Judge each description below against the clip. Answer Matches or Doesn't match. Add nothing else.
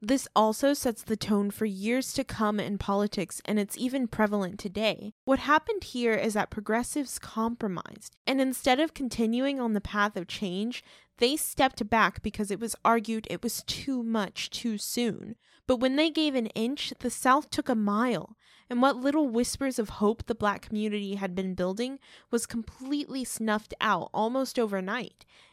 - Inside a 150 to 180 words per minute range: Matches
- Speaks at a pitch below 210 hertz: Doesn't match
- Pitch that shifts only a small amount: Doesn't match